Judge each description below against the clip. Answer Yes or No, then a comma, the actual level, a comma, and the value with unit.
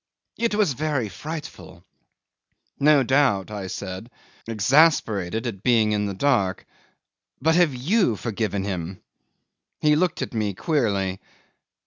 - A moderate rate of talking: No, slow, 120 wpm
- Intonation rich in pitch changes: Yes, wide, 7.3 semitones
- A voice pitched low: Yes, low, 115 Hz